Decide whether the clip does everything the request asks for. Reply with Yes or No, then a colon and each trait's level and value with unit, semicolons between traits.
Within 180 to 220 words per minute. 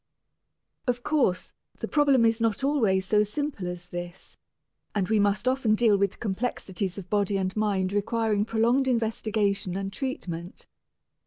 No: average, 145 wpm